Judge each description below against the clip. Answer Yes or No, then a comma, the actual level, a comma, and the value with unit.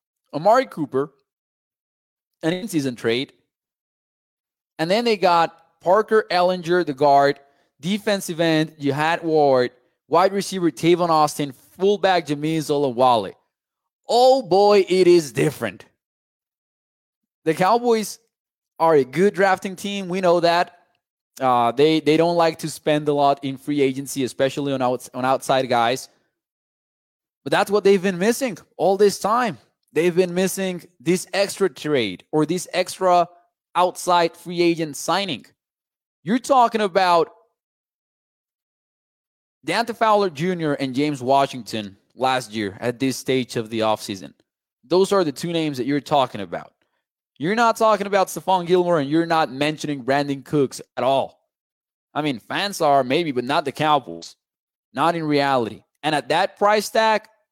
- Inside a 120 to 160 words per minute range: Yes, average, 140 wpm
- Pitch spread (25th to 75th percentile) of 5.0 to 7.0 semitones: Yes, wide, 5.5 semitones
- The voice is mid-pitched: Yes, medium, 165 Hz